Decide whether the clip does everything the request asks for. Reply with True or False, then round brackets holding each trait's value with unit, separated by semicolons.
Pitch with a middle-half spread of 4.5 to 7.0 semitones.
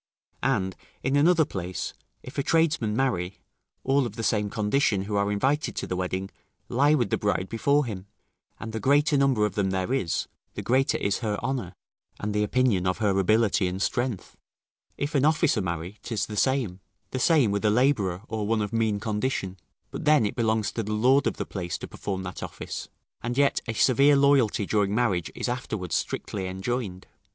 True (5.2 semitones)